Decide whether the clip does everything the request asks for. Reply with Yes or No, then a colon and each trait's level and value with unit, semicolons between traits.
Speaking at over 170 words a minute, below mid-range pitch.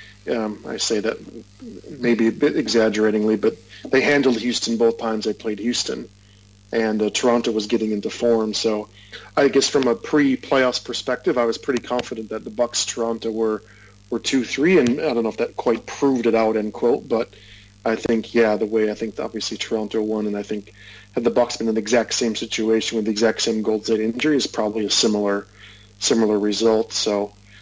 Yes: average, 200 wpm; low, 110 Hz